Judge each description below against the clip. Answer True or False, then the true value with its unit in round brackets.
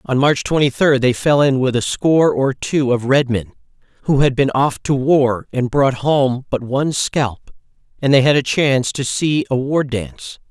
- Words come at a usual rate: False (210 wpm)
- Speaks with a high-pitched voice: False (135 Hz)